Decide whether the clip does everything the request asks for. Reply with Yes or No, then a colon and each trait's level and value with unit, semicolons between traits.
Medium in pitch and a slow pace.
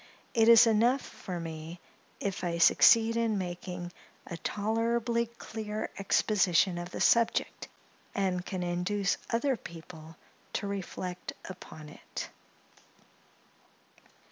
No: high, 195 Hz; slow, 110 wpm